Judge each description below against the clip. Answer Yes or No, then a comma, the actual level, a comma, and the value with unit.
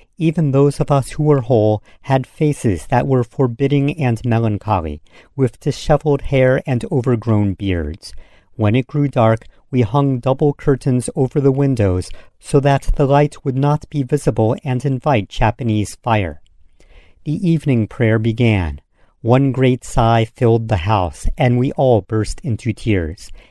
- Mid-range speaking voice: No, low, 125 Hz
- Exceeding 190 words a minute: No, average, 150 wpm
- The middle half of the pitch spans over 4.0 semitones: Yes, average, 4.8 semitones